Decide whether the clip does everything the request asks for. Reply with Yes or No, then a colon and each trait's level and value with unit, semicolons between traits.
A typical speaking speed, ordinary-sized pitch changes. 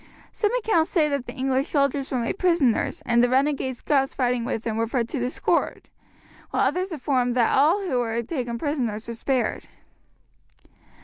Yes: average, 180 wpm; average, 3.7 semitones